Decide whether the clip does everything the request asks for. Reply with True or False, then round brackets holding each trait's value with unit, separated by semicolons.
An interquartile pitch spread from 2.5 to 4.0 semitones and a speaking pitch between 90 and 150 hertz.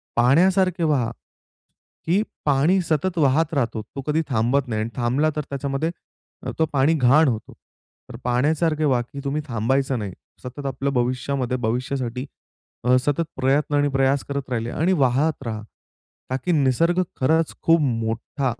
True (3.7 semitones; 135 Hz)